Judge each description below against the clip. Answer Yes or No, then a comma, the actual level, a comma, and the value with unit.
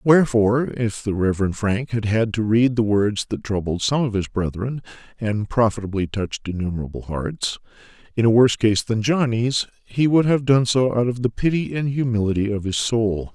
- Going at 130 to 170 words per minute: No, average, 190 wpm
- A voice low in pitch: Yes, low, 115 Hz